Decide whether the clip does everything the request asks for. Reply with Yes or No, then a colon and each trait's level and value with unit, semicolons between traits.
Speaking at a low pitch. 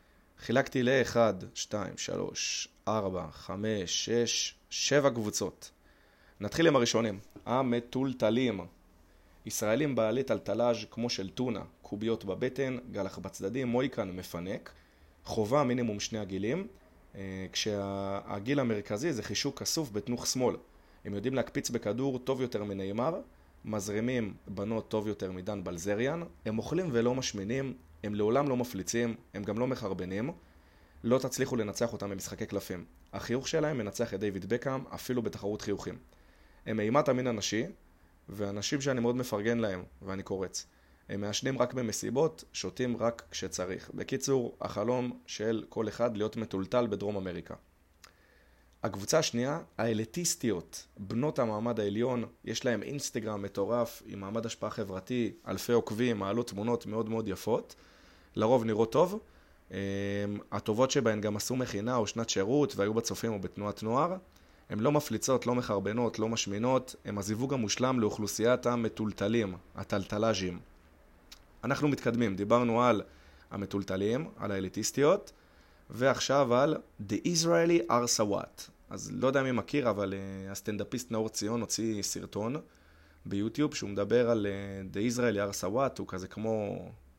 Yes: low, 110 Hz